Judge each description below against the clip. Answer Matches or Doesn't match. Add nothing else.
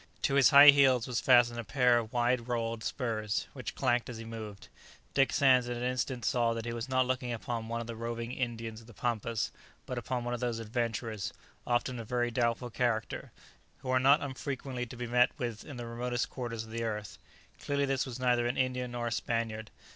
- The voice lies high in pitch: Doesn't match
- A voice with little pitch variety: Matches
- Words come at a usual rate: Doesn't match